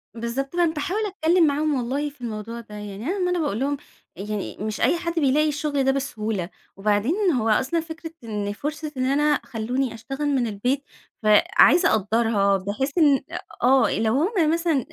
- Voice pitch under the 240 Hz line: No, very high, 270 Hz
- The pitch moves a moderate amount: No, wide, 5.9 semitones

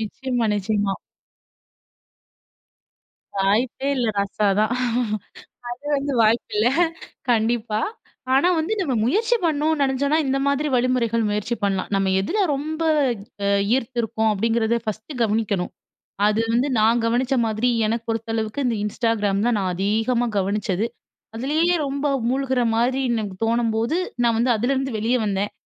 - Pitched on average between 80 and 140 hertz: No, high, 230 Hz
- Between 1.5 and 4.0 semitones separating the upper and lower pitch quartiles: Yes, average, 3.7 semitones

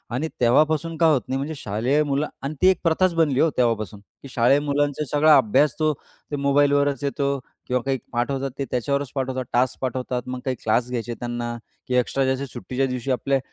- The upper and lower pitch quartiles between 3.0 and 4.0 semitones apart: No, narrow, 2.6 semitones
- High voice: No, low, 135 Hz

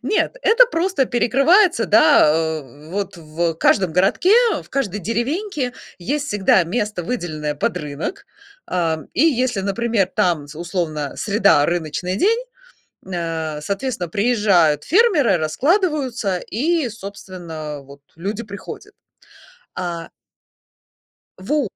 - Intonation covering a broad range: Yes, wide, 7.8 semitones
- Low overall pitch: No, high, 200 Hz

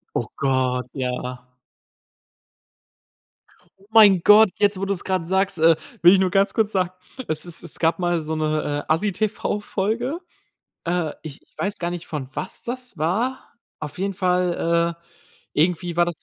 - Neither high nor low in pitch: Yes, medium, 175 Hz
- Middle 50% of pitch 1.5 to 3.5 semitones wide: No, average, 3.9 semitones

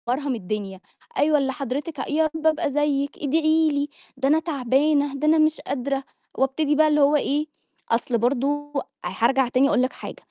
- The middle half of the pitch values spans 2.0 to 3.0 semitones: Yes, narrow, 2.5 semitones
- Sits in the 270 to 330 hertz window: Yes, very high, 285 Hz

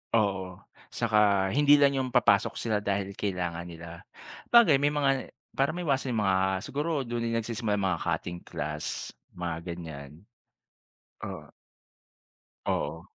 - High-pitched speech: No, low, 105 Hz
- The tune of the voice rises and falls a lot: Yes, wide, 7.6 semitones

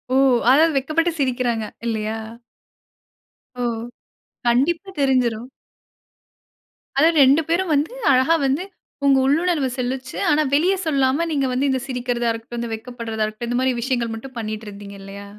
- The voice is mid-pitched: No, very high, 255 Hz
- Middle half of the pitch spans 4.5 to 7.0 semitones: No, average, 3.7 semitones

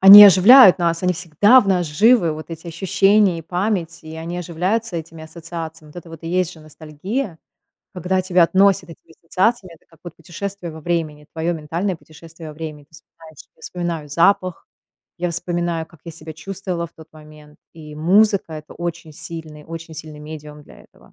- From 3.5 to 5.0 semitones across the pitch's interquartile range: No, narrow, 2.5 semitones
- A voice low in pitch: No, medium, 170 Hz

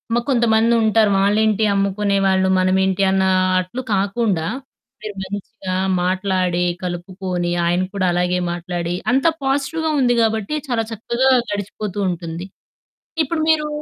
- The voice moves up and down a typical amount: Yes, average, 3.6 semitones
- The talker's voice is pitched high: Yes, high, 200 Hz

